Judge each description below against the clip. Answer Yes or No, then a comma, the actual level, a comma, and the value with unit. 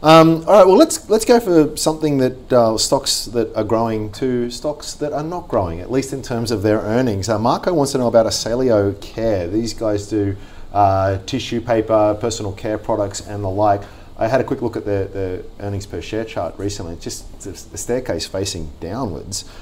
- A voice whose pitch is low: Yes, low, 110 Hz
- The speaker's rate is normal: No, fast, 210 wpm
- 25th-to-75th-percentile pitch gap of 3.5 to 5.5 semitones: Yes, average, 4.3 semitones